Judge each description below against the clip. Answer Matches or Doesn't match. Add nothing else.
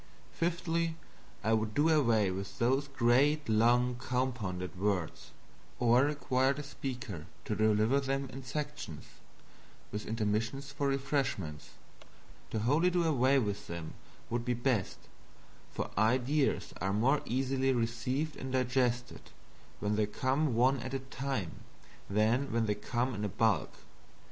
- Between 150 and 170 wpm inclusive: Doesn't match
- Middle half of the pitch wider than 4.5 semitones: Doesn't match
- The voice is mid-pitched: Doesn't match